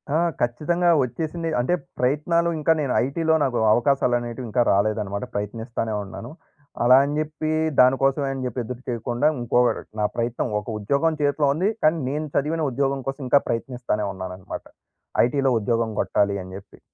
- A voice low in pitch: Yes, low, 125 Hz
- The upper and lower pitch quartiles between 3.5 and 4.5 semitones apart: Yes, average, 4.2 semitones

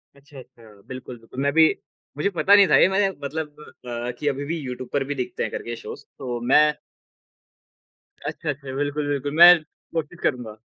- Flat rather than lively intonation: No, average, 3.4 semitones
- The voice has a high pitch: No, medium, 145 Hz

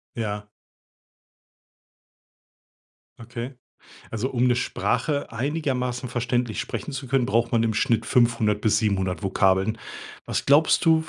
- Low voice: Yes, low, 120 Hz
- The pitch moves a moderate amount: Yes, average, 3.0 semitones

